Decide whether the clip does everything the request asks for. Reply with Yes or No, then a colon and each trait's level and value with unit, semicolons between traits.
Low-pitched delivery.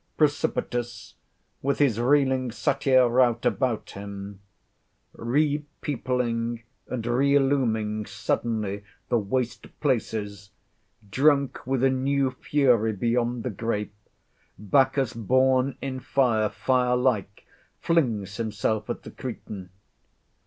Yes: low, 120 Hz